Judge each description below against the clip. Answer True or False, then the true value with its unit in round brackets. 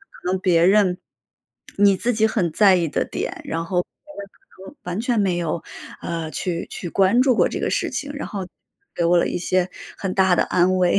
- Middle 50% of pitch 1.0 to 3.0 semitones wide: True (2.7 semitones)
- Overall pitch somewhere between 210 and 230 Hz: False (185 Hz)